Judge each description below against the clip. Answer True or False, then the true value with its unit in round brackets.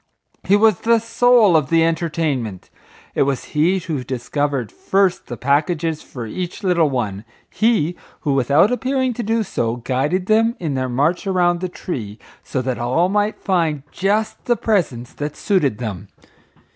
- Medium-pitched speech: True (165 Hz)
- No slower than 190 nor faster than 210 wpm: False (160 wpm)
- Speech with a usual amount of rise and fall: False (6.9 semitones)